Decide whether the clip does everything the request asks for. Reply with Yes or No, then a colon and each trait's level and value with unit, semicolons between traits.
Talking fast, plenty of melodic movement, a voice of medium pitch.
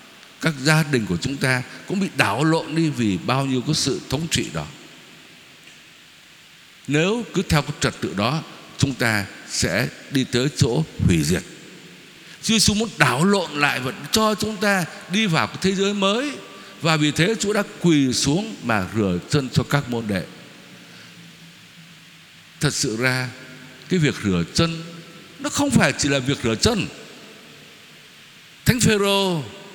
No: slow, 165 wpm; wide, 6.3 semitones; medium, 160 Hz